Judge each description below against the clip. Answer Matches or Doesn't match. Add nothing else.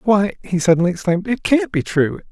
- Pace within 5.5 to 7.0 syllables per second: Matches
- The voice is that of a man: Matches